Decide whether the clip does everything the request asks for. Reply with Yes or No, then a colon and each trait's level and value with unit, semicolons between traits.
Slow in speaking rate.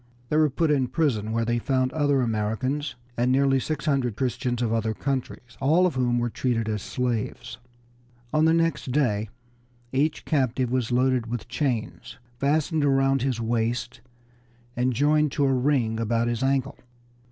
No: average, 165 wpm